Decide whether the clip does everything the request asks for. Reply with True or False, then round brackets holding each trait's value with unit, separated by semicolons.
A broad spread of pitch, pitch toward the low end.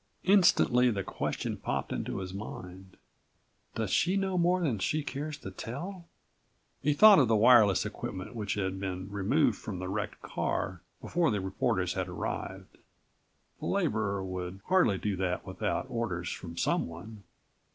True (7.6 semitones; 105 Hz)